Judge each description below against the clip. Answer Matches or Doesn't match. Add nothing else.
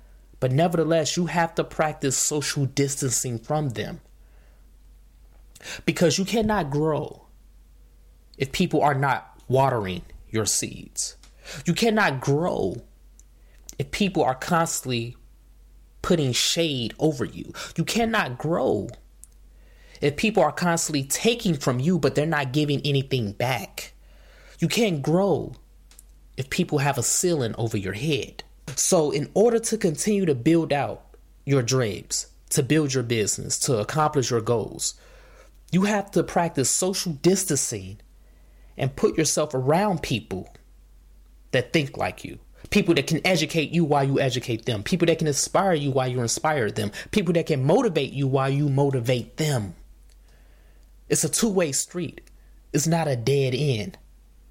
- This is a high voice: Doesn't match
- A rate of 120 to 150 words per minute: Matches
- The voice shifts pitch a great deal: Matches